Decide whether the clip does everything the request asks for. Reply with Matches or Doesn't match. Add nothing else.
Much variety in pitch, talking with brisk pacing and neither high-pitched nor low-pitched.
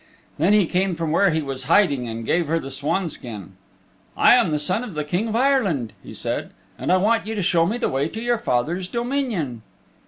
Matches